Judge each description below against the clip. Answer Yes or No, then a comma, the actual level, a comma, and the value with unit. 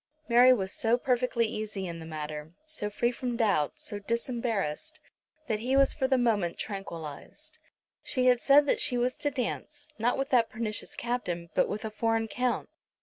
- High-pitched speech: Yes, high, 230 Hz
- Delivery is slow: No, average, 180 wpm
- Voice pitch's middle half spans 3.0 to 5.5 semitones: Yes, average, 3.9 semitones